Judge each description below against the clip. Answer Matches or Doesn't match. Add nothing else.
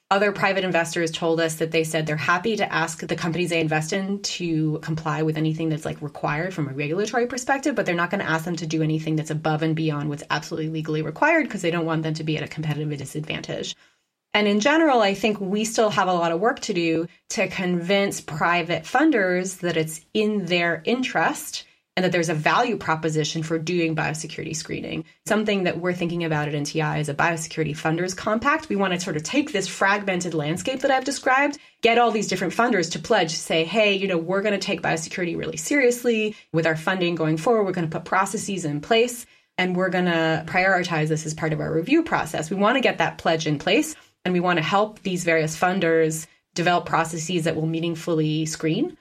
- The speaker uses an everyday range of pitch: Matches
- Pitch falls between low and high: Matches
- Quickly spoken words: Matches